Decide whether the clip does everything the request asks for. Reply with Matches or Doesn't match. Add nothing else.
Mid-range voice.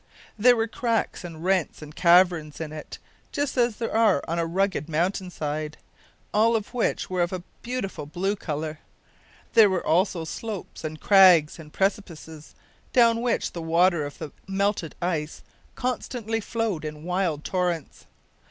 Matches